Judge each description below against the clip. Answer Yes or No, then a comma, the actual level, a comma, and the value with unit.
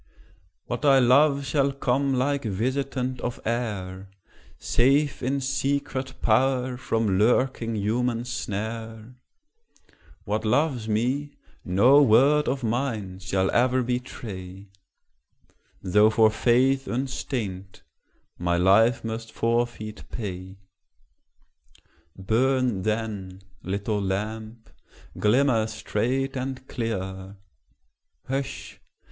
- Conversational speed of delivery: No, slow, 95 wpm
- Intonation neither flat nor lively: Yes, average, 3.9 semitones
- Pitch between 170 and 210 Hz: No, low, 115 Hz